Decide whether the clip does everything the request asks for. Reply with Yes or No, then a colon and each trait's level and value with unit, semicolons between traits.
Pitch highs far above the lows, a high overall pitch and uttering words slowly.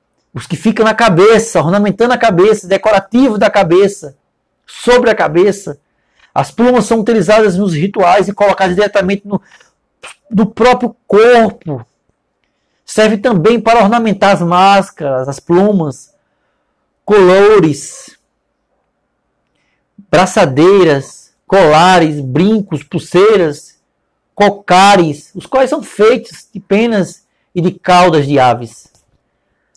No: average, 4.2 semitones; high, 200 Hz; slow, 105 wpm